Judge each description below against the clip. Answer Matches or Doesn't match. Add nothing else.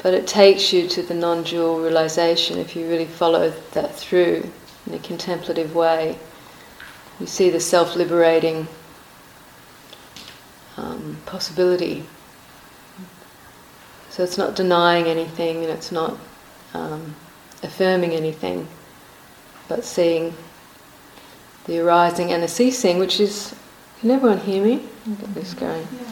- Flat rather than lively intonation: Matches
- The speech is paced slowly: Matches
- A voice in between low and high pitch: Matches